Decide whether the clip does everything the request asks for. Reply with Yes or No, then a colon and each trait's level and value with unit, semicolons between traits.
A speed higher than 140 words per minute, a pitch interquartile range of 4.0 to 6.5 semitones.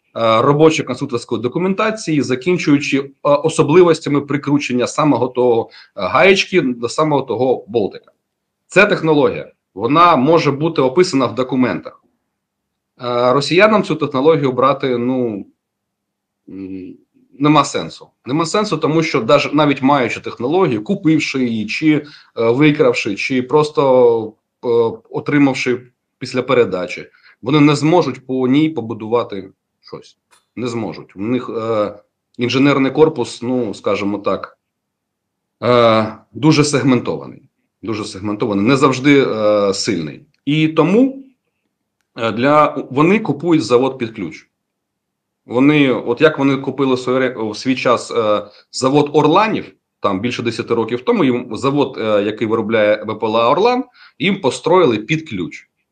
No: average, 115 wpm; average, 4.4 semitones